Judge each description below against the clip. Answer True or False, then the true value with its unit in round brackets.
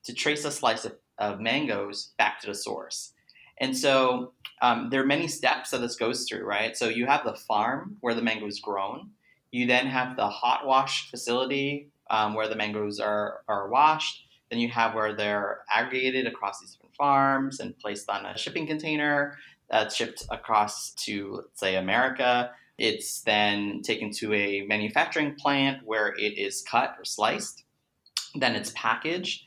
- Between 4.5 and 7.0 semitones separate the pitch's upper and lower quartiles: True (5.0 semitones)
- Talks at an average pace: True (175 wpm)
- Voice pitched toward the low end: True (125 Hz)